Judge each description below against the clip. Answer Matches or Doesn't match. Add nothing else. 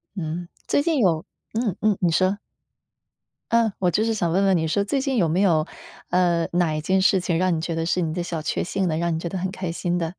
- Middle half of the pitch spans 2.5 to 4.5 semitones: Matches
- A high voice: Doesn't match